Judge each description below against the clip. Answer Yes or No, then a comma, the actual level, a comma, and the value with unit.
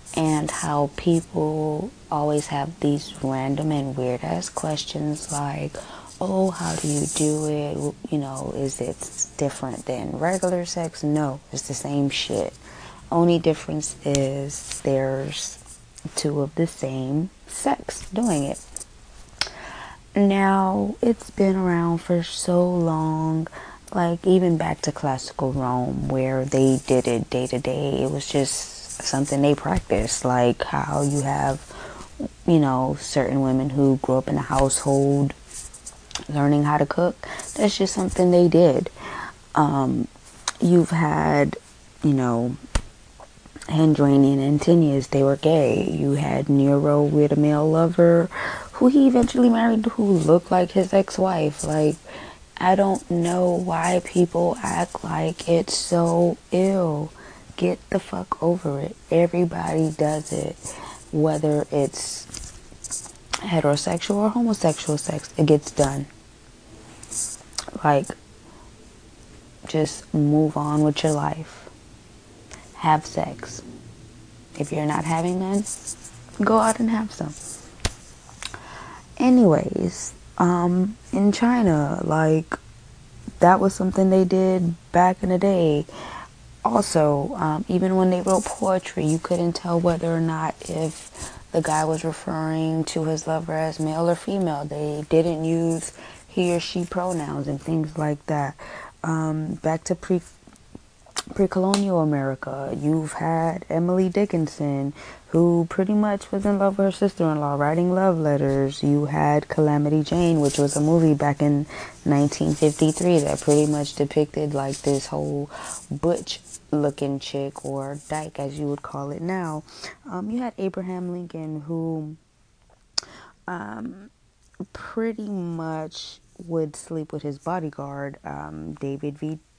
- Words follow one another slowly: Yes, slow, 130 wpm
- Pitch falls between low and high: Yes, medium, 155 Hz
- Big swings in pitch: No, average, 3.6 semitones